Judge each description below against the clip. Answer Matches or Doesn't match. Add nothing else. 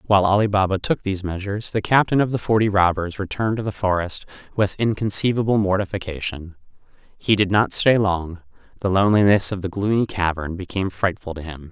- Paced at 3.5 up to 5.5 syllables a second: Doesn't match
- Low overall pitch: Matches